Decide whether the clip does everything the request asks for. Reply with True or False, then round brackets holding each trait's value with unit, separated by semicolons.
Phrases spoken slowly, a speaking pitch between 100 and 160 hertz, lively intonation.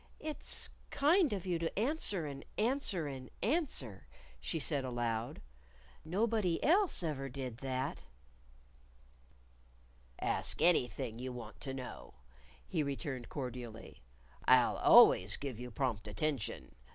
True (115 wpm; 140 Hz; 6.9 semitones)